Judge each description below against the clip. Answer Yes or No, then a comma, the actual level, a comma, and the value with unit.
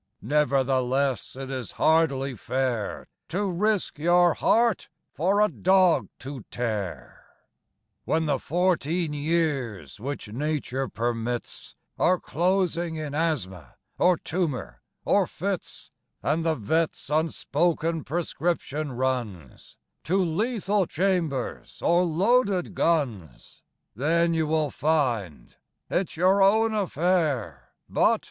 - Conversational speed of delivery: No, slow, 105 wpm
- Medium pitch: Yes, medium, 155 Hz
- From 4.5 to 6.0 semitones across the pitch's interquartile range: Yes, average, 5.2 semitones